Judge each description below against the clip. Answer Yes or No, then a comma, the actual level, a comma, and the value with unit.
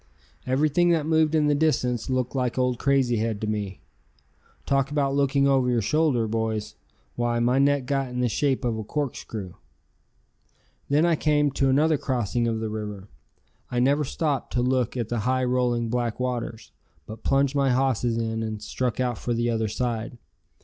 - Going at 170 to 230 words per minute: Yes, average, 180 wpm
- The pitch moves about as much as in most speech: Yes, average, 3.3 semitones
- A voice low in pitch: Yes, low, 125 Hz